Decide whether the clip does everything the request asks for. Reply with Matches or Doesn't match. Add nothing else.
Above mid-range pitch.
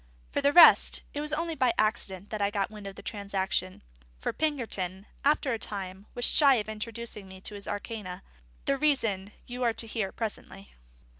Matches